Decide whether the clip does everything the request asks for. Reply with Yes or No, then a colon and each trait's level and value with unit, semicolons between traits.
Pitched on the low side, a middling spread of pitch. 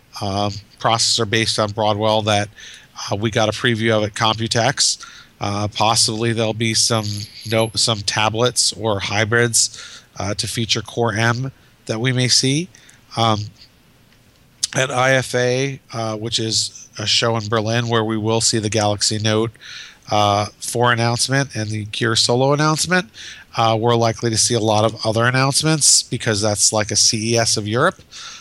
No: low, 115 Hz; narrow, 1.8 semitones